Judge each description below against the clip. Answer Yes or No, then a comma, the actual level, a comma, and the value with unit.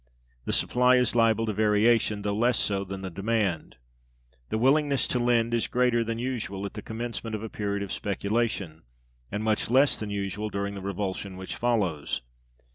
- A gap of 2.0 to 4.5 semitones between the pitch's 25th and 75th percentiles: Yes, average, 2.9 semitones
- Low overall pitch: Yes, low, 110 Hz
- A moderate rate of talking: Yes, average, 180 wpm